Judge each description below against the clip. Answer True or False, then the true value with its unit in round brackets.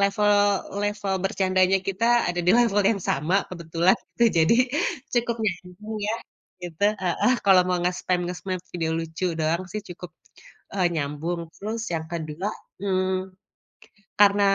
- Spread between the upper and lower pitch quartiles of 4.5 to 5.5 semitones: False (2.8 semitones)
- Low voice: False (185 Hz)